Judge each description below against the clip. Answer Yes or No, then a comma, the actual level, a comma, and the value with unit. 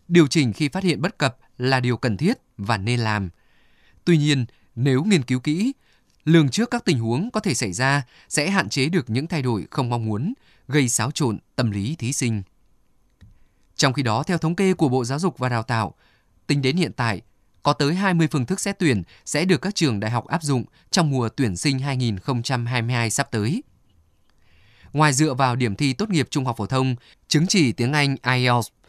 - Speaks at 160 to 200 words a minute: No, average, 210 wpm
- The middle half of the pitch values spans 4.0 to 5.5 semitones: Yes, average, 5.0 semitones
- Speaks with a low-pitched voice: Yes, low, 130 Hz